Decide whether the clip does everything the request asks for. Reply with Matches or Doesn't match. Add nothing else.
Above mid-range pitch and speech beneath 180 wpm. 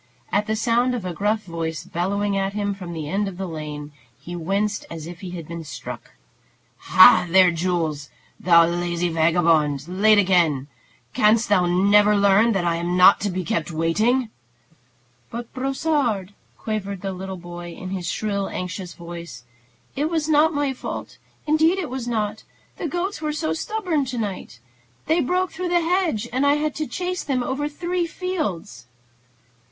Matches